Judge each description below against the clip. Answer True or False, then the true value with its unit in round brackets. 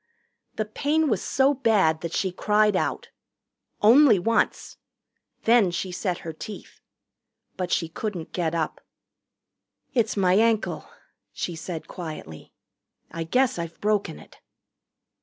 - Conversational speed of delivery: False (125 wpm)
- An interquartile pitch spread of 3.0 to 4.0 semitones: False (4.8 semitones)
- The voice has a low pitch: False (195 Hz)